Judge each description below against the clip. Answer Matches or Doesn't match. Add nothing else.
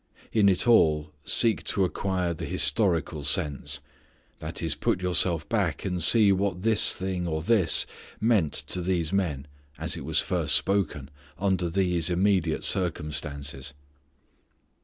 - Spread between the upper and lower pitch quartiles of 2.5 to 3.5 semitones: Doesn't match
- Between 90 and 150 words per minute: Matches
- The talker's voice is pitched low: Matches